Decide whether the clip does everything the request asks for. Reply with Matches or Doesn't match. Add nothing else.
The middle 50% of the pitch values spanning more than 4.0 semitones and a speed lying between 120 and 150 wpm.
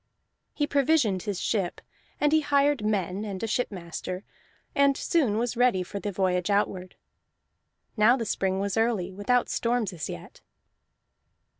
Matches